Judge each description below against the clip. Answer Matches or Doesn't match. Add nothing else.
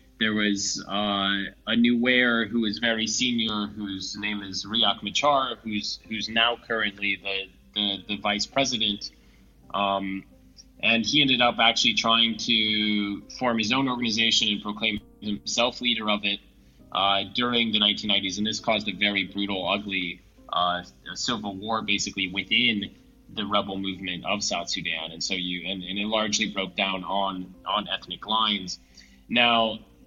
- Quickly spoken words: Doesn't match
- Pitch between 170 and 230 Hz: Doesn't match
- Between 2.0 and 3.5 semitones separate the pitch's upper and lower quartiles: Matches